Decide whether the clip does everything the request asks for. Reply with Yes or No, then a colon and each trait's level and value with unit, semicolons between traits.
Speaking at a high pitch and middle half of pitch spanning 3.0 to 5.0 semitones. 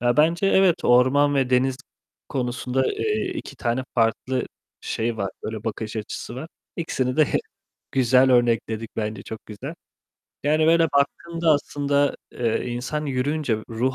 No: low, 130 Hz; average, 3.7 semitones